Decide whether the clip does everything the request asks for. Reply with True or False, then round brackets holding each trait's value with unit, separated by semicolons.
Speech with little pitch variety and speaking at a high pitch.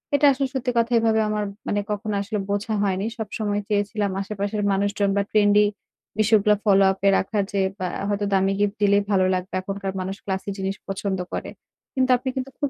True (1.6 semitones; 205 Hz)